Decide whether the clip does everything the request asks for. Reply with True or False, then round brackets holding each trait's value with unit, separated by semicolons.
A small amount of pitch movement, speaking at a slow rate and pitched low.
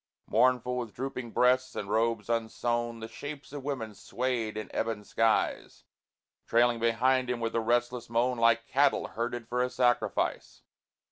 False (1.8 semitones; 150 wpm; 120 Hz)